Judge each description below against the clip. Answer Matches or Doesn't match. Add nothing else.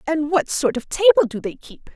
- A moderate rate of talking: Doesn't match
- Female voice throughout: Matches